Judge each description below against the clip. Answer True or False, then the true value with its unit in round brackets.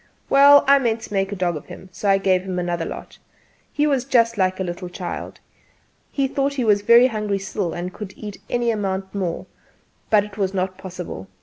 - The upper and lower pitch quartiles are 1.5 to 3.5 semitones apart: False (3.9 semitones)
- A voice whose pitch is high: True (200 Hz)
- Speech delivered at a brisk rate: True (210 wpm)